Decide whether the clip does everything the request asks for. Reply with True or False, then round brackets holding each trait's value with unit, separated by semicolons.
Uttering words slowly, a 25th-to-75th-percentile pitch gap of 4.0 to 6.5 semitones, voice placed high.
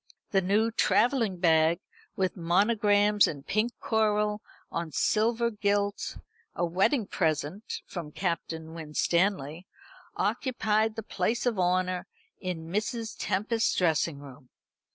True (110 wpm; 4.3 semitones; 195 Hz)